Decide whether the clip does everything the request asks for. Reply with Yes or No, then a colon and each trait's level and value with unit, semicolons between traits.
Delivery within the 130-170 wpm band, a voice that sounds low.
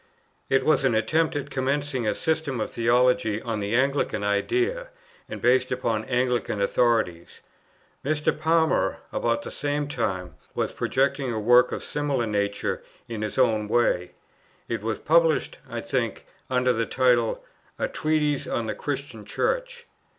Yes: average, 150 wpm; low, 125 Hz